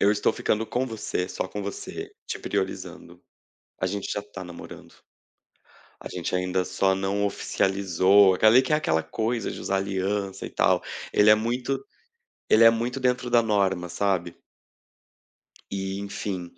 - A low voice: Yes, low, 100 Hz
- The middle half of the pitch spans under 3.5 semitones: Yes, average, 2.9 semitones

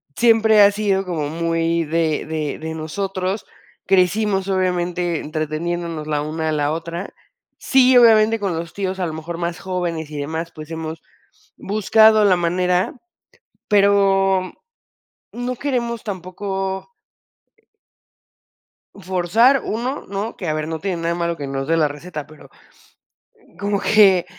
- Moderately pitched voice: Yes, medium, 180 Hz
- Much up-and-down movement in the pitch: No, average, 3.8 semitones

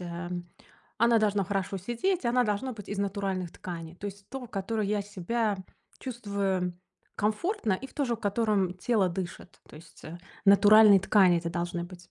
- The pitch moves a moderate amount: Yes, average, 3.4 semitones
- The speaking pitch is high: Yes, high, 200 Hz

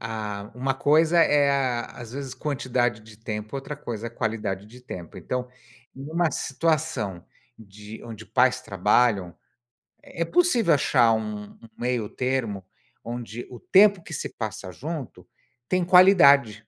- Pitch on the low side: Yes, low, 125 Hz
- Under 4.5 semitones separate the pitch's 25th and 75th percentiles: No, average, 5.0 semitones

